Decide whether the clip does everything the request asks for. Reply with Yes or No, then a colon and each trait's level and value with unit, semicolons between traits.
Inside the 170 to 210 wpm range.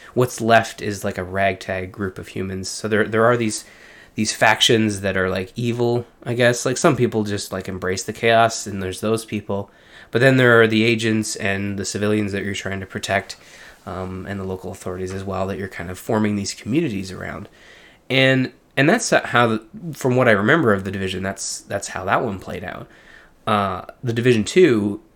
Yes: fast, 205 wpm